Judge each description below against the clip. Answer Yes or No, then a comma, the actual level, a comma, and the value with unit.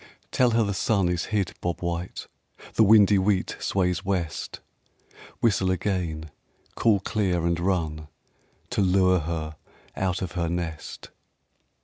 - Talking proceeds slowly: Yes, slow, 130 wpm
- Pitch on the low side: Yes, very low, 90 Hz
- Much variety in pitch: No, narrow, 2.6 semitones